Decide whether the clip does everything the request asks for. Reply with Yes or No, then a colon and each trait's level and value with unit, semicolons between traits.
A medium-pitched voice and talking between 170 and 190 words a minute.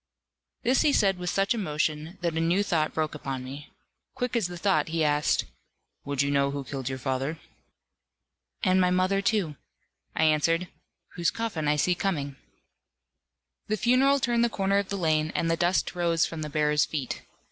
Yes: medium, 165 Hz; average, 180 wpm